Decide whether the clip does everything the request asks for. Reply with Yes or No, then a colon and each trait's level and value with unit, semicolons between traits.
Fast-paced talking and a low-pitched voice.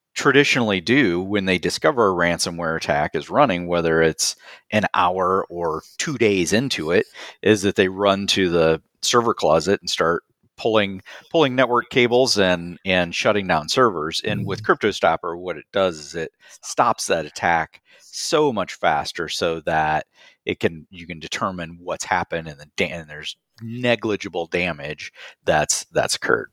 No: average, 160 wpm; very low, 90 Hz